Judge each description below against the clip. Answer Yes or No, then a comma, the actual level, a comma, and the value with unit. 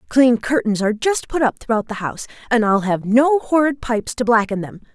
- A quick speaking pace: Yes, fast, 220 wpm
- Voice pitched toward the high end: Yes, high, 240 Hz